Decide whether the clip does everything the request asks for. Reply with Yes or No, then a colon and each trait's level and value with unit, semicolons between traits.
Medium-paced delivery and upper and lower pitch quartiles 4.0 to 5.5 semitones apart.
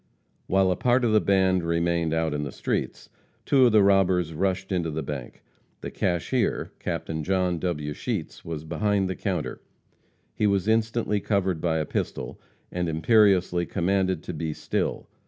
No: average, 165 wpm; average, 3.3 semitones